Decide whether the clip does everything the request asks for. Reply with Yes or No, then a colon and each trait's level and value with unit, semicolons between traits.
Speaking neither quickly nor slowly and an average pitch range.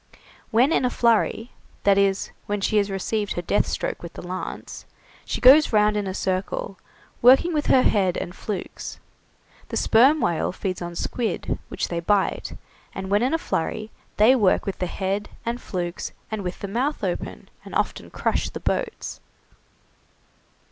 Yes: average, 170 wpm; average, 4.2 semitones